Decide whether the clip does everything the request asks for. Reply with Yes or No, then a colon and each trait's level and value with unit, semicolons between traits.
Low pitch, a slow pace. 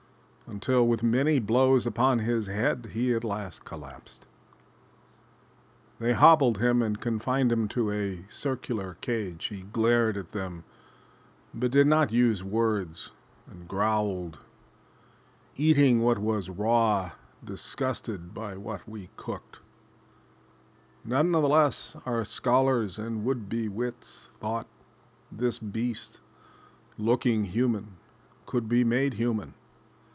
Yes: low, 115 Hz; slow, 115 wpm